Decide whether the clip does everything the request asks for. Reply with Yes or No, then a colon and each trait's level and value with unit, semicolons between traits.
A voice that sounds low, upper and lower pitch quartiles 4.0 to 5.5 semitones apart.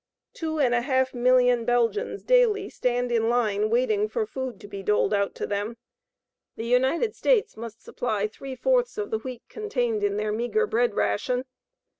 No: high, 245 Hz; average, 4.4 semitones